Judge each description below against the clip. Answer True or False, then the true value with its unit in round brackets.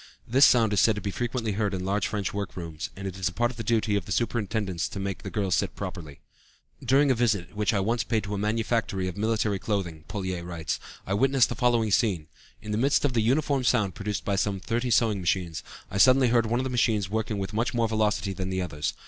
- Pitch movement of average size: True (3.4 semitones)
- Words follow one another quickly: True (250 wpm)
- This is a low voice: True (105 Hz)